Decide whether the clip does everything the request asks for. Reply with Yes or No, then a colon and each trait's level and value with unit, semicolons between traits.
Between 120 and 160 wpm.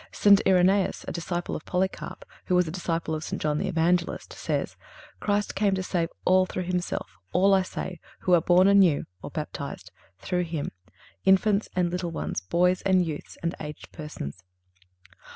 No: average, 170 wpm